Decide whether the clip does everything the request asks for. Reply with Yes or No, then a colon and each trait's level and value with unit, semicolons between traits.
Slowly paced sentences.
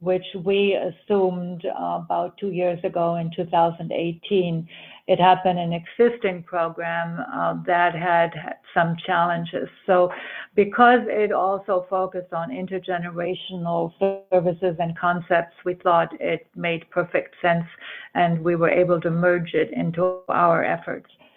Yes: slow, 125 wpm